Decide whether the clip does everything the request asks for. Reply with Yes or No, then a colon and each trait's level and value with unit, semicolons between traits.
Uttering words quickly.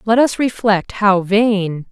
No: average, 155 wpm